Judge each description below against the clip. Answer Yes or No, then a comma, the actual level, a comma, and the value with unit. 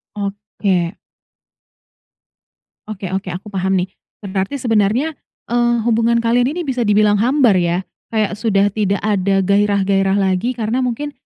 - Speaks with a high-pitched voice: Yes, high, 205 Hz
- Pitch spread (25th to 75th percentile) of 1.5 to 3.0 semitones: No, average, 3.4 semitones